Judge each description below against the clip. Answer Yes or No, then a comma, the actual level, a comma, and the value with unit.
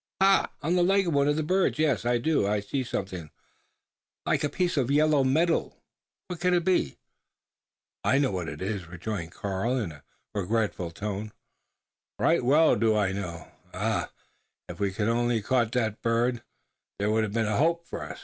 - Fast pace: No, average, 190 wpm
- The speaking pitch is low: Yes, low, 115 Hz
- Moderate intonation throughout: No, wide, 7.1 semitones